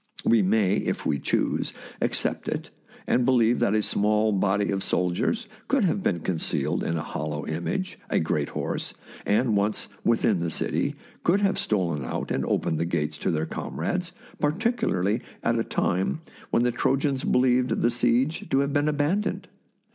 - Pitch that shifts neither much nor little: No, wide, 7.5 semitones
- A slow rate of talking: No, average, 175 wpm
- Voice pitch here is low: Yes, low, 110 Hz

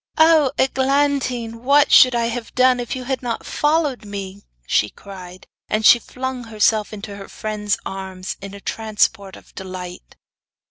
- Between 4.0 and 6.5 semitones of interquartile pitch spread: Yes, average, 4.5 semitones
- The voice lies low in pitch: No, high, 225 Hz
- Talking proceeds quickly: No, average, 155 wpm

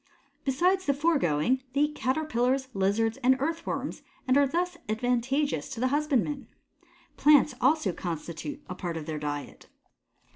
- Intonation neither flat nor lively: No, wide, 6.7 semitones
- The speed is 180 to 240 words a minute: No, average, 140 wpm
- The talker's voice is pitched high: Yes, very high, 260 Hz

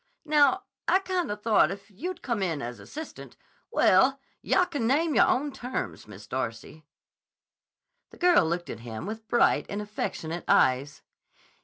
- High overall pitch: Yes, high, 220 Hz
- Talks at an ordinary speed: Yes, average, 145 wpm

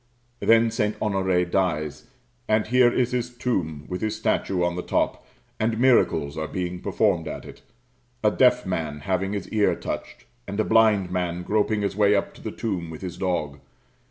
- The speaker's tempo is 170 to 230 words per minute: Yes, average, 185 wpm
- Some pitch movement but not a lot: Yes, average, 3.7 semitones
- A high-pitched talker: No, low, 100 Hz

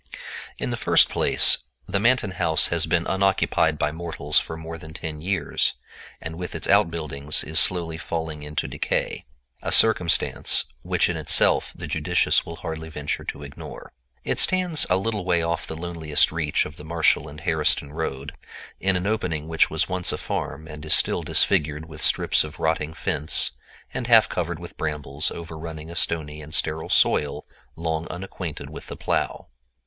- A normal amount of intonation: No, narrow, 2.2 semitones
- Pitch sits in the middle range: No, very low, 80 Hz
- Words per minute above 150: Yes, average, 170 wpm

